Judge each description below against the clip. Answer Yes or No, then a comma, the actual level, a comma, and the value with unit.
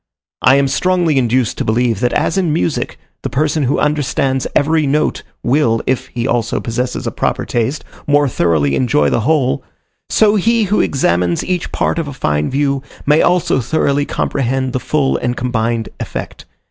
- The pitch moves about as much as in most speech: Yes, average, 4.1 semitones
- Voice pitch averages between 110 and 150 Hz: Yes, low, 135 Hz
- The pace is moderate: Yes, average, 170 wpm